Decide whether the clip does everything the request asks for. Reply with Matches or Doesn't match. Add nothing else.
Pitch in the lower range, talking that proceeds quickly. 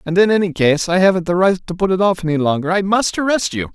Doesn't match